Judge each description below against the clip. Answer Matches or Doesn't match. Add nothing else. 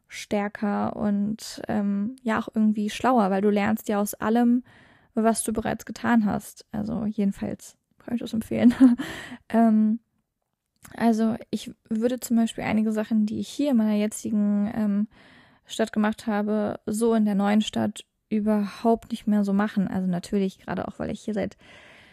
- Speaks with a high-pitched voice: Matches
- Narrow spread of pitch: Matches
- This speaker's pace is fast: Doesn't match